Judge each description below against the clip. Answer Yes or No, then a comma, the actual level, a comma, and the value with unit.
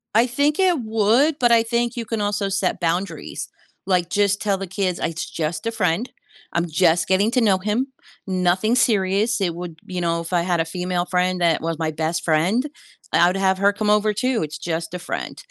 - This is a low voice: No, high, 190 Hz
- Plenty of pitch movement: No, average, 4.3 semitones